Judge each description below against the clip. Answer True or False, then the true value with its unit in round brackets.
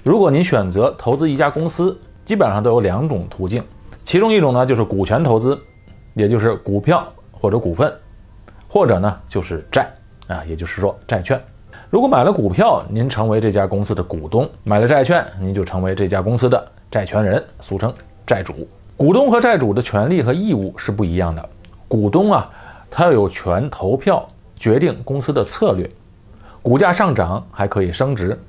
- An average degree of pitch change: True (4.1 semitones)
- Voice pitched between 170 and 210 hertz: False (105 Hz)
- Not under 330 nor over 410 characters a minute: False (275 characters per minute)